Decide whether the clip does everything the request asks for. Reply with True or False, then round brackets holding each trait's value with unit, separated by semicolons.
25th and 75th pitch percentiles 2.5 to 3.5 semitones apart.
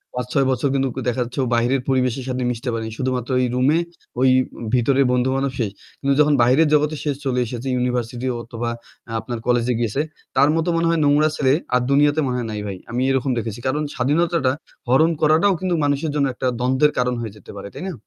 True (2.9 semitones)